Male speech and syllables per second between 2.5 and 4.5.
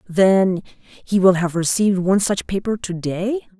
No: female; 4.3 syllables/s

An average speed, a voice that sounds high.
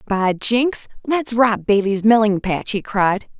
Yes: average, 160 wpm; high, 215 Hz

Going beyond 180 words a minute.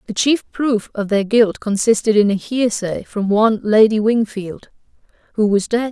No: average, 170 wpm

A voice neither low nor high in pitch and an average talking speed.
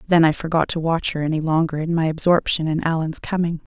No: medium, 160 Hz; fast, 225 wpm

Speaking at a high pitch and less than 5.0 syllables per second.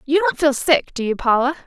No: very high, 290 Hz; 5.5 syllables/s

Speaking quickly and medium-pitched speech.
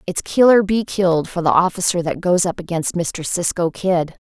Yes: fast, 210 wpm; medium, 180 Hz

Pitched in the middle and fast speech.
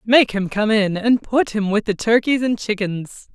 No: high, 215 Hz; fast, 215 wpm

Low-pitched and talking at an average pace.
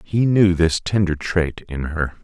Yes: very low, 85 Hz; average, 190 wpm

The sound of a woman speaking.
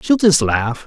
No: male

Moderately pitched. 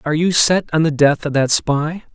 Yes: medium, 155 Hz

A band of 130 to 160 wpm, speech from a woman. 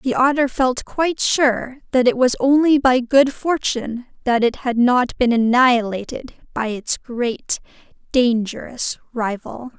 Yes: average, 140 wpm; female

